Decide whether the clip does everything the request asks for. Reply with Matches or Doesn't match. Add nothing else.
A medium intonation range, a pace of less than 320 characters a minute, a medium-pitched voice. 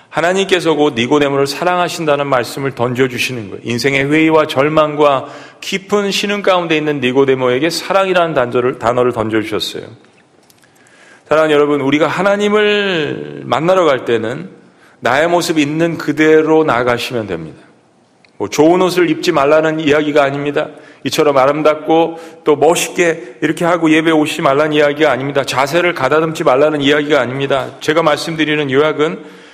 Doesn't match